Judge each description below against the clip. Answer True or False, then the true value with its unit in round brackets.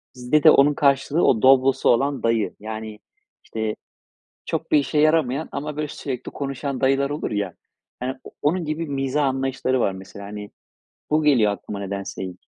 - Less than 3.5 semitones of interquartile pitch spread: False (5.0 semitones)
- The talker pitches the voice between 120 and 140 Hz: True (135 Hz)